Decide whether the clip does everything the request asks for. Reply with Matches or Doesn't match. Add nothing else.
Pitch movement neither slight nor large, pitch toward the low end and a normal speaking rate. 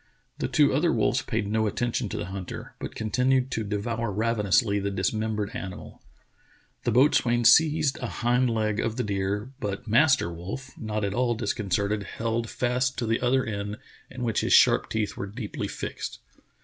Matches